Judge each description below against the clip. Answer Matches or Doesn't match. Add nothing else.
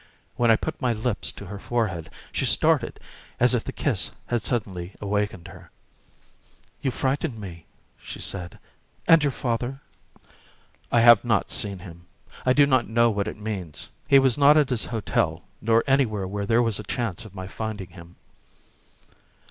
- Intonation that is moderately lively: Matches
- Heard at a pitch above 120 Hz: Doesn't match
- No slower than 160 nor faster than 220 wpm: Matches